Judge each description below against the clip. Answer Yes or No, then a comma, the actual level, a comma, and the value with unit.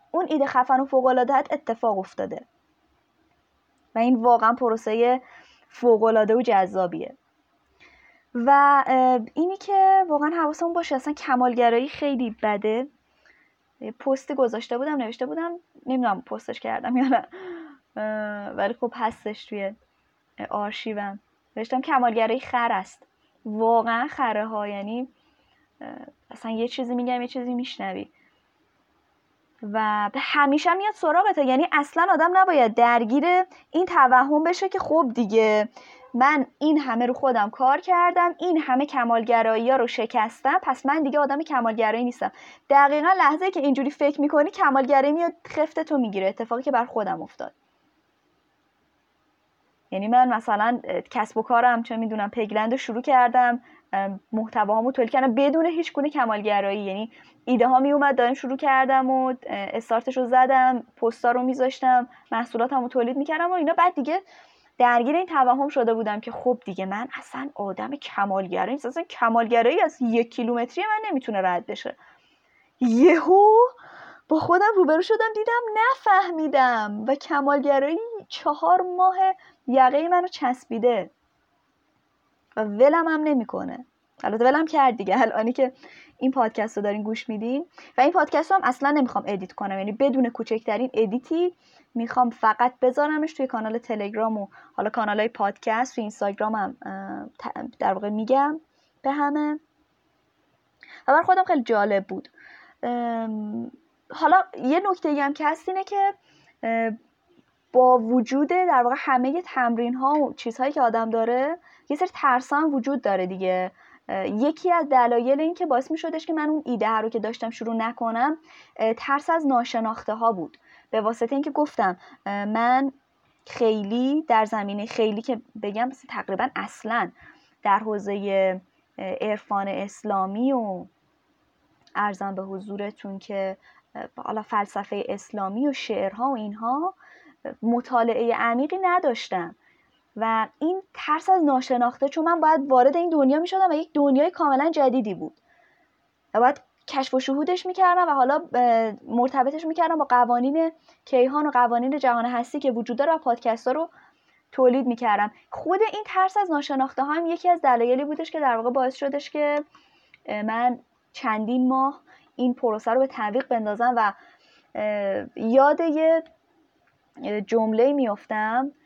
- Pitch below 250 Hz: No, very high, 255 Hz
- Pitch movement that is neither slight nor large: Yes, average, 4.8 semitones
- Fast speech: No, average, 140 wpm